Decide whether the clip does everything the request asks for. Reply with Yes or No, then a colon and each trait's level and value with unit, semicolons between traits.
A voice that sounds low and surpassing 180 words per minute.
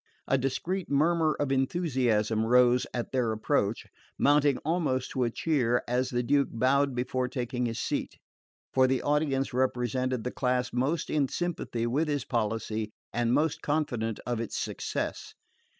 No: low, 130 Hz; average, 150 wpm